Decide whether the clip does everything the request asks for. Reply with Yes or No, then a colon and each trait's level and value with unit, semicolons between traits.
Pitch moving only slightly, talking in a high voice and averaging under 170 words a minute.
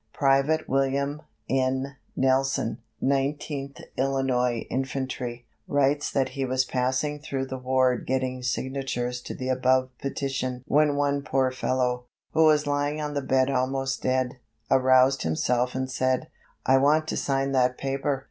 No: narrow, 1.3 semitones; low, 130 Hz; average, 140 wpm